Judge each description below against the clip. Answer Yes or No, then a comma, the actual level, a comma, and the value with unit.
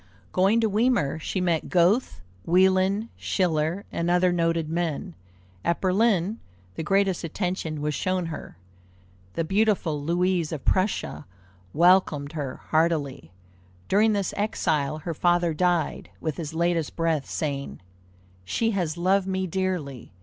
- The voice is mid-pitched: Yes, medium, 175 Hz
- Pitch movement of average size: Yes, average, 3.3 semitones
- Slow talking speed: Yes, slow, 130 wpm